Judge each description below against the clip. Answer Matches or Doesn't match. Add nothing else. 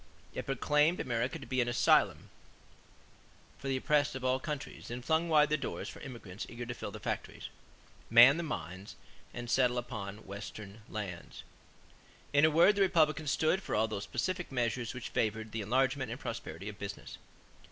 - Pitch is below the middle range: Matches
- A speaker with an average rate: Matches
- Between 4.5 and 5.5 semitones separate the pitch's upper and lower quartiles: Matches